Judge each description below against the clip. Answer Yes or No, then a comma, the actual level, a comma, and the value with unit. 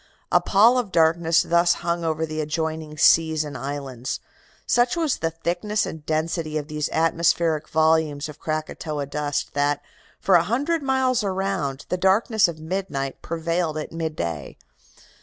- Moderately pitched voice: Yes, medium, 160 Hz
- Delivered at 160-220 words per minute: No, average, 150 wpm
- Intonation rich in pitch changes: No, average, 3.2 semitones